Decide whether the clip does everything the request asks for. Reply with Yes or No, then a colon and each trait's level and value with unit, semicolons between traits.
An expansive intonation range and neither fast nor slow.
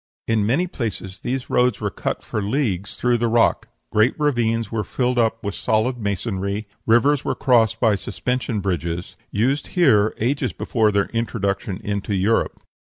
No: average, 3.4 semitones; average, 155 wpm